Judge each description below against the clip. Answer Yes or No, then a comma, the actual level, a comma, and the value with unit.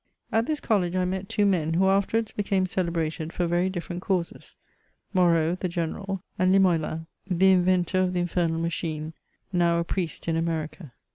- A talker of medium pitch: Yes, medium, 180 Hz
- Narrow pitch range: Yes, narrow, 2.2 semitones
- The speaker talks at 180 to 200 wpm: No, average, 165 wpm